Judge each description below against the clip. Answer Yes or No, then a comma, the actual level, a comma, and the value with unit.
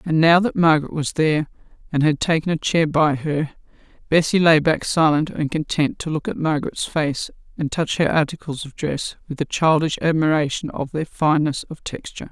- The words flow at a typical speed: Yes, average, 190 wpm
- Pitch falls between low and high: Yes, medium, 155 Hz